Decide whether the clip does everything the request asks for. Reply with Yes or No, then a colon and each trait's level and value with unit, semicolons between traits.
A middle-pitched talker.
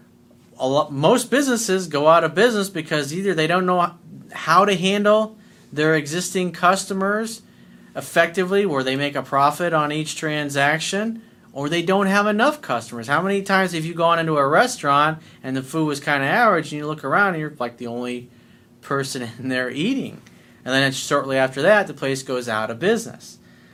Yes: medium, 160 Hz